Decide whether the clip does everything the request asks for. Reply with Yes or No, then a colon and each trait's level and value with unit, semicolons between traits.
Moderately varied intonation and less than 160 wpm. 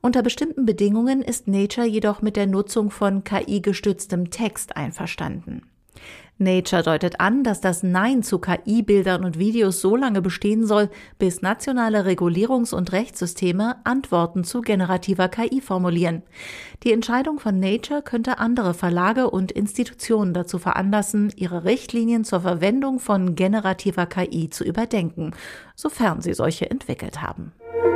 Yes: average, 3.9 semitones; average, 135 wpm